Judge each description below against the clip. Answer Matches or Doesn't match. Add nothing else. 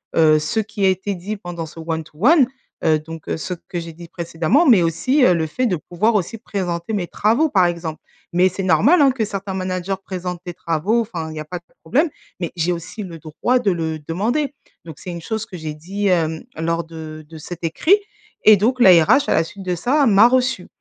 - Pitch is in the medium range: Matches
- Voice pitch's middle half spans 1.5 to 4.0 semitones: Doesn't match